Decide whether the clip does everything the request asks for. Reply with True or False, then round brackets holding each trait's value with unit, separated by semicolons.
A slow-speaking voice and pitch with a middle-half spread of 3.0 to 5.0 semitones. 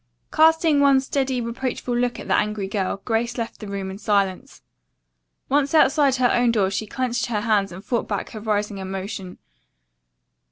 False (170 wpm; 4.4 semitones)